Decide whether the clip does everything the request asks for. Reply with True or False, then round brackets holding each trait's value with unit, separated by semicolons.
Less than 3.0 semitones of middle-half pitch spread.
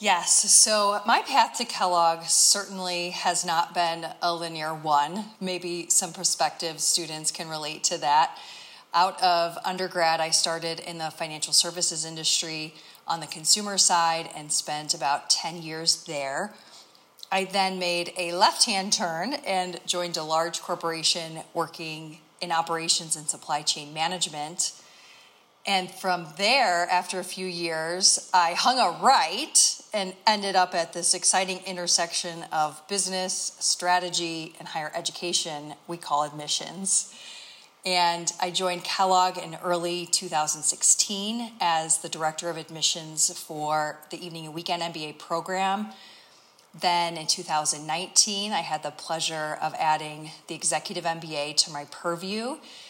True (2.5 semitones)